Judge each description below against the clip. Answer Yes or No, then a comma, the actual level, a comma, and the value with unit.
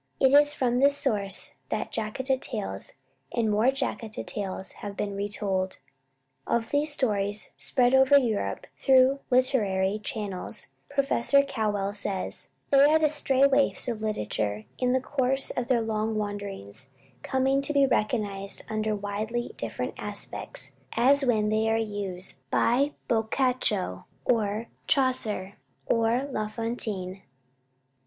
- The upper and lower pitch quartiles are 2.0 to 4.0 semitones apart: No, average, 4.4 semitones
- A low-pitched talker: No, high, 225 Hz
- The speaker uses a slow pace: Yes, slow, 130 wpm